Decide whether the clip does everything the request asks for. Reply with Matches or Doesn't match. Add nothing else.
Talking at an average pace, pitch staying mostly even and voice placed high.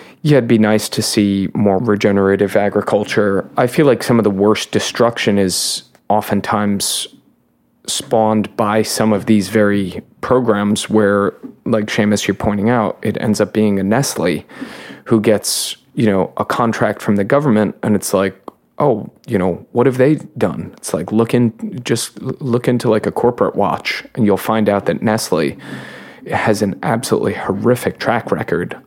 Doesn't match